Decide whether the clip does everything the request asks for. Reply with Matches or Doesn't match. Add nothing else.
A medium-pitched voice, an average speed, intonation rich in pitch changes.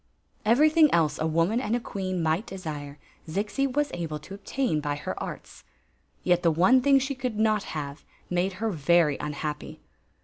Matches